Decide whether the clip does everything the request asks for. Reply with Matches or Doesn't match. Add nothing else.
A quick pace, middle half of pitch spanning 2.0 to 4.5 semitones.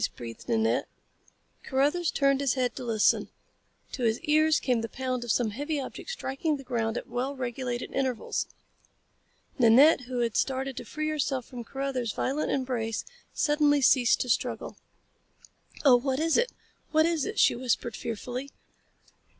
Doesn't match